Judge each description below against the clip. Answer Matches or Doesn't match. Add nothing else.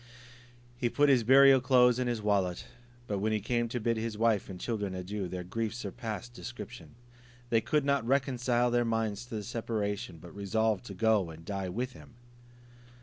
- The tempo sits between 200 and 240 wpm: Doesn't match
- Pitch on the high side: Doesn't match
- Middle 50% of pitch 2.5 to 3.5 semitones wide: Matches